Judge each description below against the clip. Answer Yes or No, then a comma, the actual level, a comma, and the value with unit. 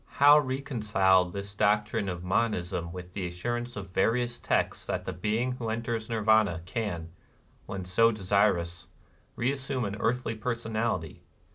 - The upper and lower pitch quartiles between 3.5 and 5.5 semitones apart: Yes, average, 4.3 semitones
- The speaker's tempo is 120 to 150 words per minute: Yes, average, 140 wpm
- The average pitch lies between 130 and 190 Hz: No, low, 105 Hz